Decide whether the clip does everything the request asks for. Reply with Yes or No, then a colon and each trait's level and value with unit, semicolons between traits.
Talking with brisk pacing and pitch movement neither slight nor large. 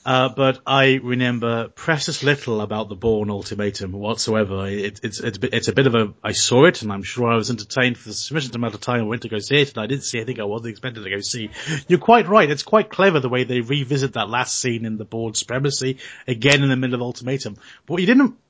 Yes: fast, 260 wpm; average, 3.9 semitones